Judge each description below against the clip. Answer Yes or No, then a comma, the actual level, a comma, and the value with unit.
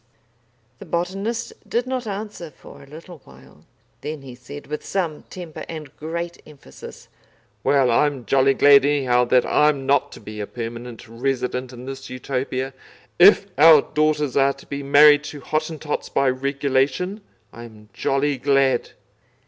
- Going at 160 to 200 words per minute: No, average, 150 wpm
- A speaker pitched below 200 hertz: Yes, medium, 140 Hz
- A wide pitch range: No, average, 3.3 semitones